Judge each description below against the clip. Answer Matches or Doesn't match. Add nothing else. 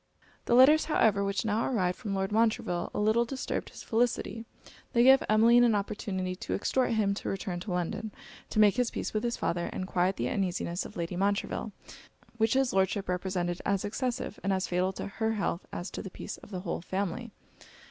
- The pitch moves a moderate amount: Matches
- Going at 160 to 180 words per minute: Doesn't match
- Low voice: Doesn't match